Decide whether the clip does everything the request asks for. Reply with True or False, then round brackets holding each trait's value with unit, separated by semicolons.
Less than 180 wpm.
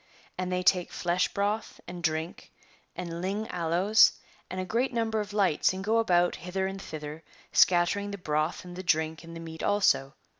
False (185 wpm)